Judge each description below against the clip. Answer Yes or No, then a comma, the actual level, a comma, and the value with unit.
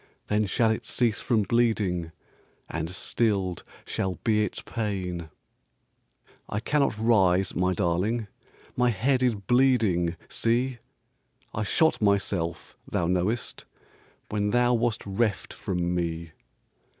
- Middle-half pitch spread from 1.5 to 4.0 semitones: No, average, 4.6 semitones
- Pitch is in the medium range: No, low, 105 Hz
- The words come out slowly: Yes, slow, 115 wpm